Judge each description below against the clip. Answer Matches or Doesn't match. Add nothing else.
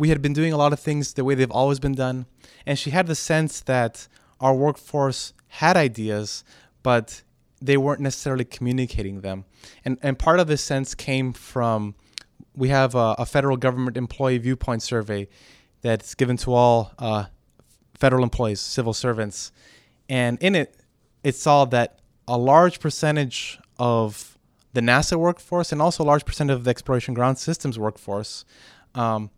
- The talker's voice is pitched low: Matches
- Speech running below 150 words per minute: Doesn't match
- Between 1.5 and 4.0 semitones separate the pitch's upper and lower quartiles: Matches